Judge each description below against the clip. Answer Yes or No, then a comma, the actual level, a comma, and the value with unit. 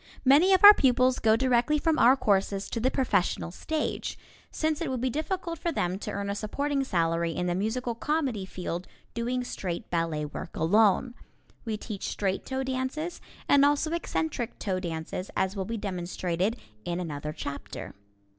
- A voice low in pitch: No, high, 225 Hz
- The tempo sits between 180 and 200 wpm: No, average, 170 wpm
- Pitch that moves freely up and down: Yes, wide, 6.8 semitones